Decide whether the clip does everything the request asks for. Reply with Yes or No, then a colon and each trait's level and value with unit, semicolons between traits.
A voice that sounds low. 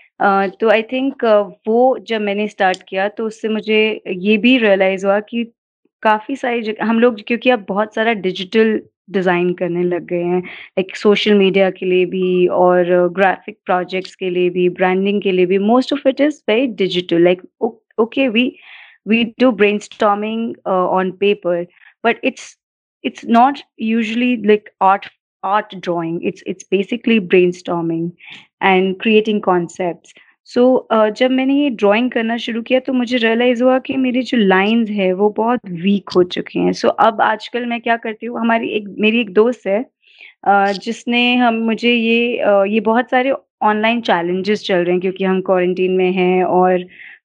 No: high, 210 Hz